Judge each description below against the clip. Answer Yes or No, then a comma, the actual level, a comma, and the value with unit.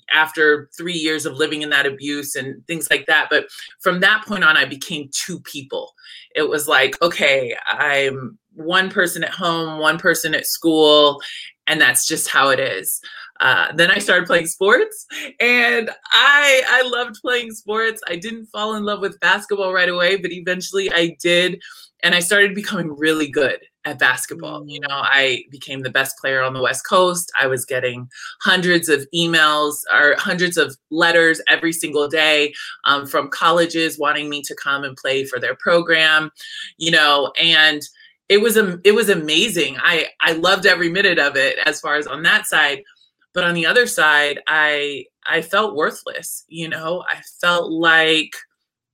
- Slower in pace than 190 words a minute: Yes, average, 180 wpm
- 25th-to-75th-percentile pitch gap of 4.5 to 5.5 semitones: Yes, average, 4.9 semitones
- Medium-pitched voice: Yes, medium, 170 Hz